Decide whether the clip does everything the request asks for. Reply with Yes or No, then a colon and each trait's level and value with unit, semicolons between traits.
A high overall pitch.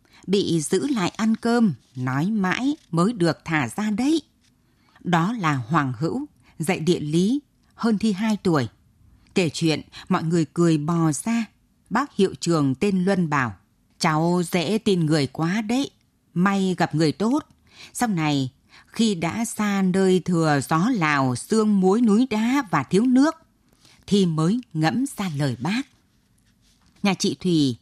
No: medium, 180 Hz